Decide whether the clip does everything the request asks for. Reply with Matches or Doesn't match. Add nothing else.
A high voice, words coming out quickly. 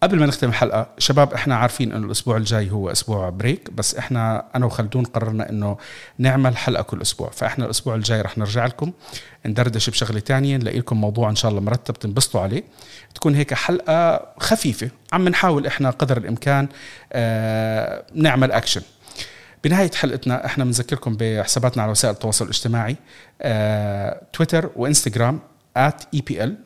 Doesn't match